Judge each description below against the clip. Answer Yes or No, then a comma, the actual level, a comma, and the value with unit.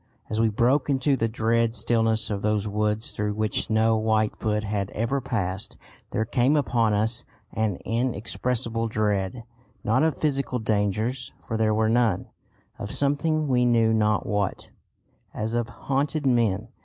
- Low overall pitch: Yes, low, 110 Hz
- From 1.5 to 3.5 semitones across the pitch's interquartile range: Yes, narrow, 2.5 semitones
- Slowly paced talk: No, average, 155 wpm